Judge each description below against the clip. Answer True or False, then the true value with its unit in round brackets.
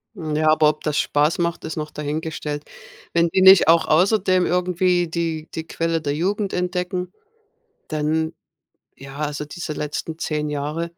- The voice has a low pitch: False (160 Hz)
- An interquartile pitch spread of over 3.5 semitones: False (2.8 semitones)